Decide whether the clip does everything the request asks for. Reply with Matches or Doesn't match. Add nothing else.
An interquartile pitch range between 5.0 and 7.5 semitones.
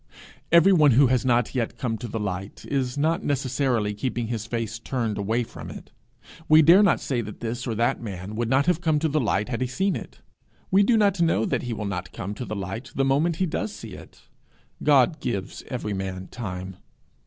Matches